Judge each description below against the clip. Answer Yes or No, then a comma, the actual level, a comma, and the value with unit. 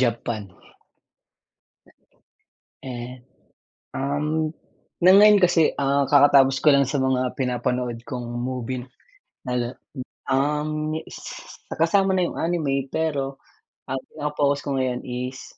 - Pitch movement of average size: Yes, average, 3.3 semitones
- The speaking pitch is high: No, low, 135 Hz